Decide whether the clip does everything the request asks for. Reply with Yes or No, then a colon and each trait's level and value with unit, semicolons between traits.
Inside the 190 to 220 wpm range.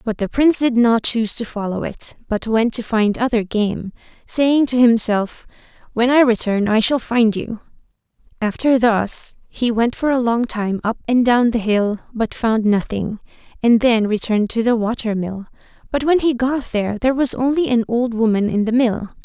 Yes: average, 195 wpm